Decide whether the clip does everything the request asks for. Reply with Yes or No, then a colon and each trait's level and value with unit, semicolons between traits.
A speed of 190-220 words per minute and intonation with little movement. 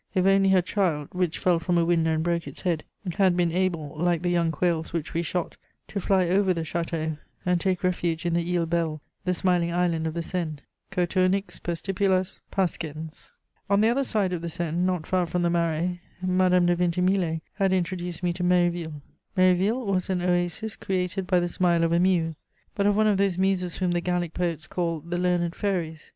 Yes: fast, 205 wpm; narrow, 1.7 semitones